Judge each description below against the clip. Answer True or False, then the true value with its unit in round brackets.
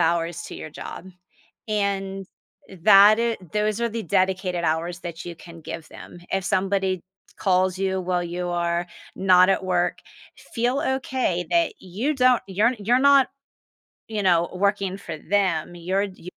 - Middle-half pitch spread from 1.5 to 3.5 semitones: True (3.2 semitones)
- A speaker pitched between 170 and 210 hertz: True (190 Hz)